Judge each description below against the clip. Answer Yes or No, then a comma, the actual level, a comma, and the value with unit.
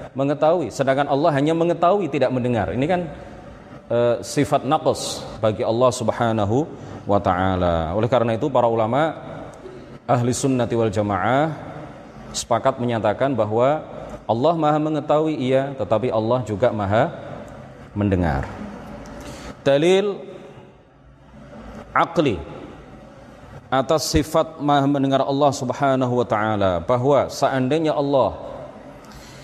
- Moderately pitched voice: No, low, 130 Hz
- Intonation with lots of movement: No, average, 4.3 semitones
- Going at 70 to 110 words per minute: Yes, average, 105 wpm